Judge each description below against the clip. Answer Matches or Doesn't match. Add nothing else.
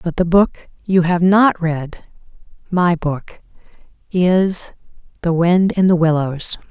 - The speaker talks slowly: Matches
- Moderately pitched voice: Matches